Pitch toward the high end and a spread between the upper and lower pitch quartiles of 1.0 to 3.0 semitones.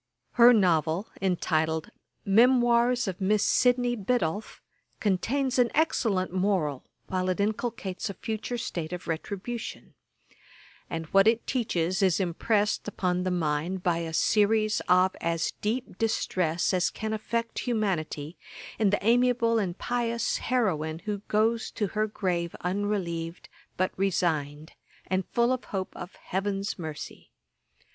No: high, 195 Hz; average, 4.3 semitones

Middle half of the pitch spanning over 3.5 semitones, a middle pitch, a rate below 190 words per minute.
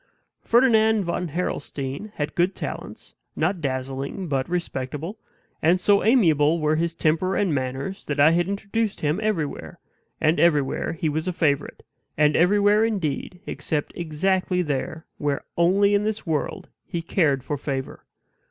Yes: average, 4.8 semitones; medium, 165 Hz; average, 145 wpm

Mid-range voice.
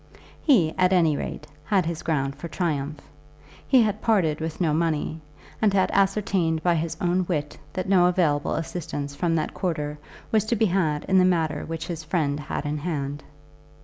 Yes: medium, 165 Hz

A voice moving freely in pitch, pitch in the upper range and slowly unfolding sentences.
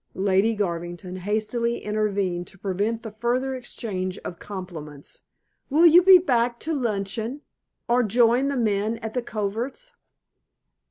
No: average, 4.0 semitones; high, 220 Hz; slow, 130 wpm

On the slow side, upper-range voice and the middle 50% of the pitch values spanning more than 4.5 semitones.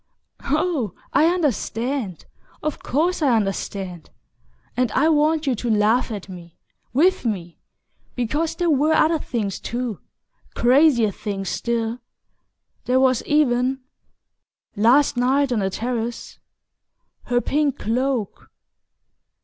Yes: slow, 110 wpm; high, 245 Hz; average, 5.0 semitones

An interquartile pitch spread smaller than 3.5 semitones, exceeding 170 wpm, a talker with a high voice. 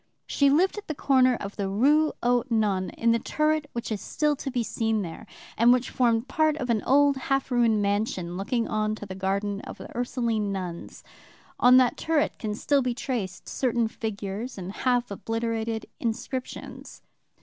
No: average, 3.8 semitones; average, 180 wpm; high, 230 Hz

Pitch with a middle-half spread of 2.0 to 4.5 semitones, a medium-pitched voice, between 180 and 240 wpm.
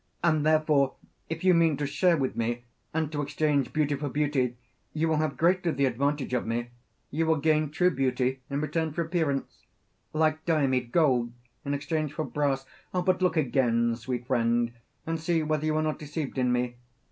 Yes: average, 3.4 semitones; medium, 145 Hz; average, 185 wpm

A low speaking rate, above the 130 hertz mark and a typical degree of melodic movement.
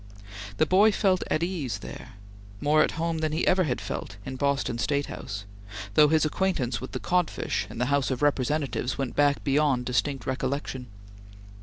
No: average, 175 wpm; medium, 140 Hz; average, 3.6 semitones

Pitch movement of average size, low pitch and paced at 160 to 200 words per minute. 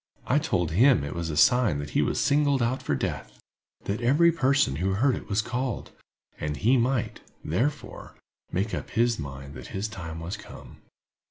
No: wide, 8.1 semitones; low, 110 Hz; average, 180 wpm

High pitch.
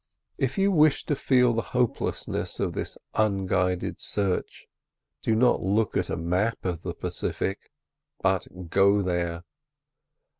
No: low, 100 Hz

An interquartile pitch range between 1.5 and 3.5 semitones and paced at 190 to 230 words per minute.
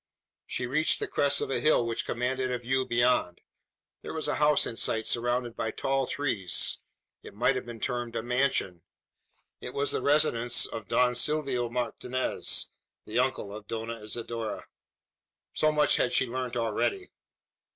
No: average, 2.7 semitones; average, 160 wpm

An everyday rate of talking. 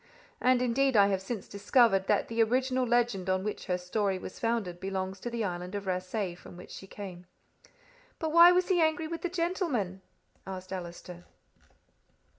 Yes: average, 175 wpm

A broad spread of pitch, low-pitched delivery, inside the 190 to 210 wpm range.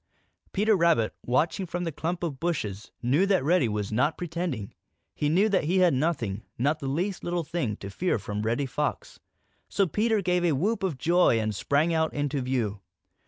No: wide, 6.3 semitones; medium, 155 Hz; average, 195 wpm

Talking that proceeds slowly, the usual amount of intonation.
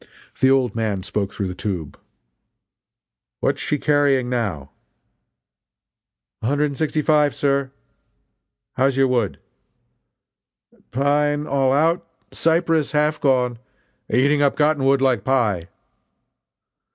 Yes: slow, 115 wpm; average, 3.8 semitones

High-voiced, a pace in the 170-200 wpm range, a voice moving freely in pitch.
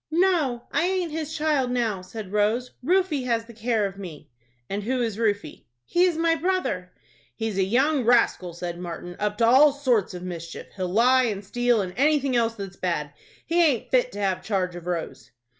Yes: high, 230 Hz; average, 195 wpm; wide, 6.5 semitones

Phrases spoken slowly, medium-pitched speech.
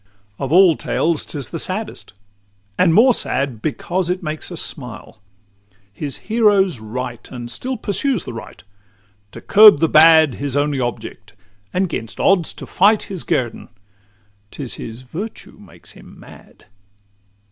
No: average, 155 wpm; medium, 155 Hz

